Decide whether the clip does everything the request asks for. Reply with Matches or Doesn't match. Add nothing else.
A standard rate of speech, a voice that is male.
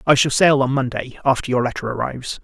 Doesn't match